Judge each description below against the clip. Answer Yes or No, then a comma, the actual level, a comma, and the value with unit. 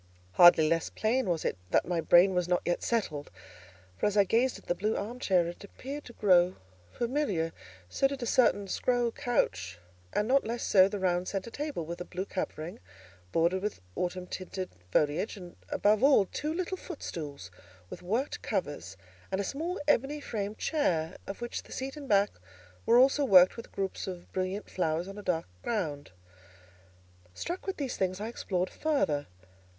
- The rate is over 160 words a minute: Yes, average, 180 wpm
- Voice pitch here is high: Yes, high, 195 Hz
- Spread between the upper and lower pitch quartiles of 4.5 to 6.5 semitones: Yes, wide, 5.6 semitones